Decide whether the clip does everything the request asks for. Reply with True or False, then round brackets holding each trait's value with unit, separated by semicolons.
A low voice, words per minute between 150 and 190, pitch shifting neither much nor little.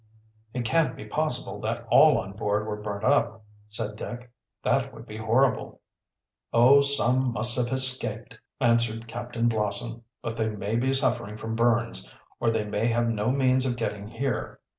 False (115 Hz; 165 wpm; 2.3 semitones)